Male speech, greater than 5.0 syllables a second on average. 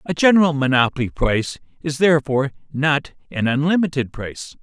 Yes: male; 5.9 syllables/s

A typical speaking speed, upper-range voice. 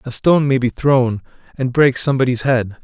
No: average, 190 wpm; low, 130 Hz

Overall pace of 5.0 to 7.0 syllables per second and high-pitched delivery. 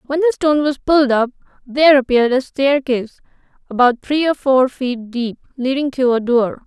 Yes: 5.4 syllables/s; very high, 265 Hz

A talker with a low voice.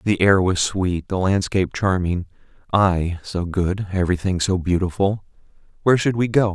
Yes: very low, 95 Hz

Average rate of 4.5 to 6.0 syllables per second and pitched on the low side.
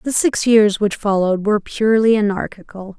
No: 5.6 syllables/s; high, 210 Hz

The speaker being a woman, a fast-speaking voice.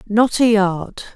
No: female; average, 155 wpm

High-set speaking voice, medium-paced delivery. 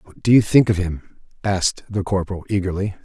No: very low, 95 Hz; average, 195 wpm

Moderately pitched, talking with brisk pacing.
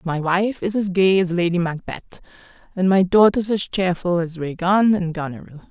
No: medium, 180 Hz; average, 180 wpm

